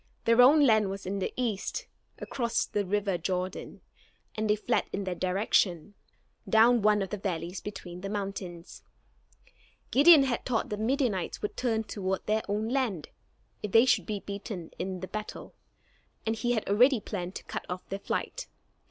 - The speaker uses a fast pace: No, average, 175 wpm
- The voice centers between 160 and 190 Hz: No, high, 210 Hz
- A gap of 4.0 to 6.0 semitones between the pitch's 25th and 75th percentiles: No, average, 3.3 semitones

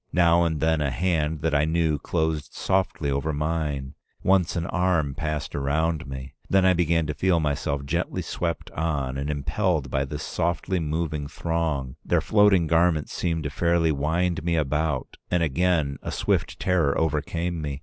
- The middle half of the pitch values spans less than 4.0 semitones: Yes, average, 2.8 semitones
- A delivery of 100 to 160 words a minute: No, average, 170 wpm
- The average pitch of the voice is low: Yes, very low, 80 Hz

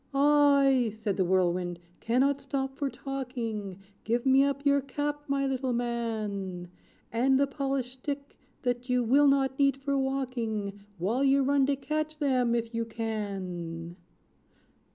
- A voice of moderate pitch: No, very high, 255 Hz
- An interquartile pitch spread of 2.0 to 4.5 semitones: Yes, average, 3.9 semitones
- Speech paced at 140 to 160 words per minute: Yes, average, 145 wpm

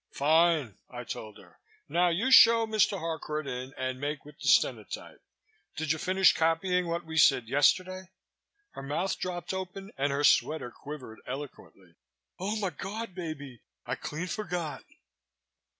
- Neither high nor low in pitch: Yes, medium, 160 Hz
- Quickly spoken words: No, average, 140 wpm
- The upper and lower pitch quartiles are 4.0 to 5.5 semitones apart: Yes, average, 4.9 semitones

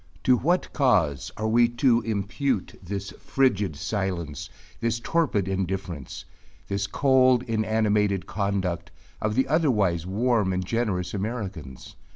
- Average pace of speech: No, slow, 120 wpm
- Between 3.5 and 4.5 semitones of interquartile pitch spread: Yes, average, 4.2 semitones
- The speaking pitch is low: Yes, low, 105 Hz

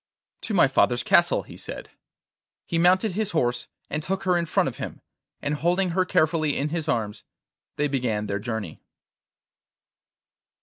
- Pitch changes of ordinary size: No, wide, 6.6 semitones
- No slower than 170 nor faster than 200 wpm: No, average, 160 wpm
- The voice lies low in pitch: No, medium, 155 Hz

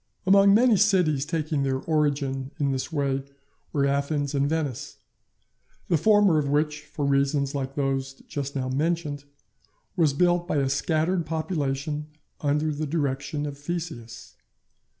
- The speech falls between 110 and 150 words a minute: Yes, average, 140 wpm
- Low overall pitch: No, medium, 145 Hz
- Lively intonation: No, average, 2.7 semitones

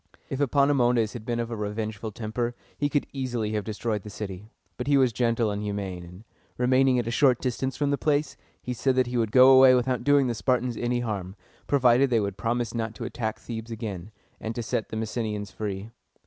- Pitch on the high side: No, low, 115 Hz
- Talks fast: Yes, fast, 215 wpm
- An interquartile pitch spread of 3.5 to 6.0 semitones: No, average, 3.0 semitones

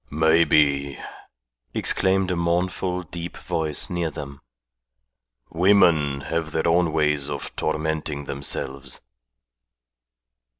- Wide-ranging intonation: No, average, 3.1 semitones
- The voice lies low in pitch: Yes, very low, 80 Hz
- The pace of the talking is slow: Yes, slow, 90 wpm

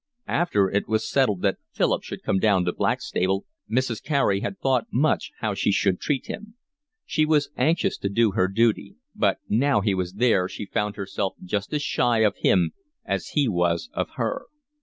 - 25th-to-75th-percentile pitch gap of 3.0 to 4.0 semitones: No, average, 5.1 semitones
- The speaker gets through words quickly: No, average, 185 wpm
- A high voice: No, low, 105 Hz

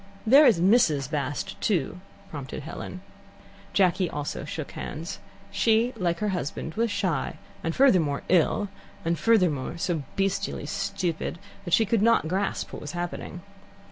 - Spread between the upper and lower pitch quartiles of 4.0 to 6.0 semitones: Yes, average, 4.5 semitones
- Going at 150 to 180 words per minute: No, average, 140 wpm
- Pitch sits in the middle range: Yes, medium, 180 Hz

